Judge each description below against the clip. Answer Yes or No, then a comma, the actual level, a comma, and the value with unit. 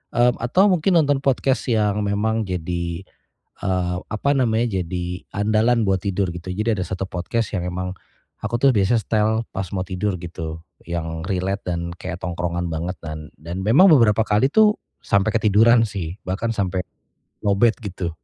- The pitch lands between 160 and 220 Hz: No, low, 100 Hz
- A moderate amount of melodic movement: Yes, average, 4.3 semitones